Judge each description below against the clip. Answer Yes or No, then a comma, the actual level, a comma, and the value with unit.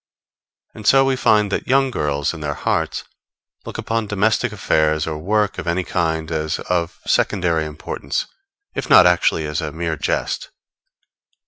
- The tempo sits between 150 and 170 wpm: Yes, average, 155 wpm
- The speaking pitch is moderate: No, very low, 85 Hz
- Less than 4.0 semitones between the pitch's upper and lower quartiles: No, average, 5.0 semitones